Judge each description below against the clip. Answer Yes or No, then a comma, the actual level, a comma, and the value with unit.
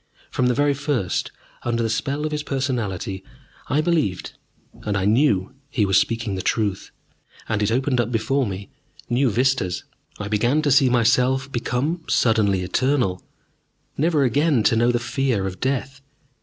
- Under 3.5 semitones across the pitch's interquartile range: No, average, 4.8 semitones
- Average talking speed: Yes, average, 160 wpm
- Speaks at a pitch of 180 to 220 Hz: No, low, 120 Hz